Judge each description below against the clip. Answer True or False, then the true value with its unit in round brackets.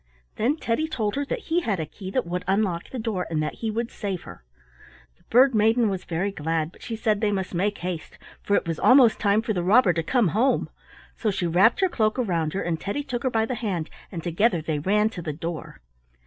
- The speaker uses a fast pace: True (240 wpm)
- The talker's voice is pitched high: True (205 Hz)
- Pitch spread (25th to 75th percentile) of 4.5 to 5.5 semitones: True (5.0 semitones)